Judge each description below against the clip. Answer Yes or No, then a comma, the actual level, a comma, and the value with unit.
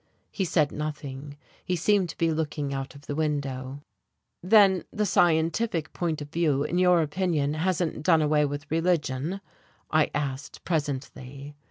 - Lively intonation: No, average, 3.2 semitones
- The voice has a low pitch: No, medium, 155 Hz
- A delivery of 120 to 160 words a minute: Yes, average, 150 wpm